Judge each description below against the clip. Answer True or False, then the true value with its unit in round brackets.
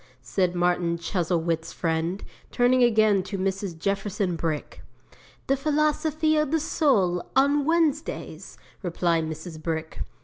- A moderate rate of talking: False (115 wpm)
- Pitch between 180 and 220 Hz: True (190 Hz)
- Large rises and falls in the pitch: True (8.3 semitones)